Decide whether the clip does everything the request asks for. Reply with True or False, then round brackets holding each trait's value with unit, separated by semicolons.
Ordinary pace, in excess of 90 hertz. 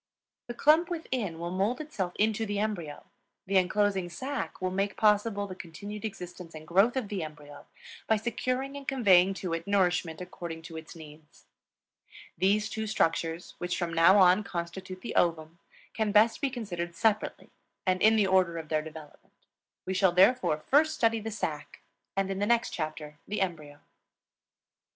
True (170 wpm; 190 Hz)